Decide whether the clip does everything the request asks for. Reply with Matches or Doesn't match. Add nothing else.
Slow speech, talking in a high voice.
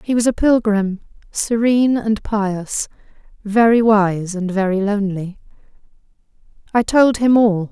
Matches